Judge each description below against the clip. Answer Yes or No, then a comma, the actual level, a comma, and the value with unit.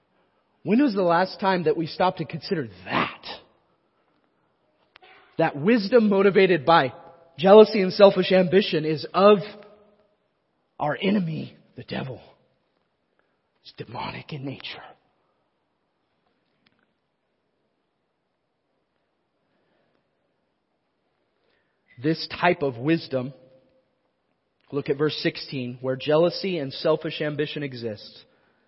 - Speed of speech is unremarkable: No, slow, 90 wpm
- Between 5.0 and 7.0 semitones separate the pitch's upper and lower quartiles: Yes, average, 5.3 semitones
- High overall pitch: No, medium, 165 Hz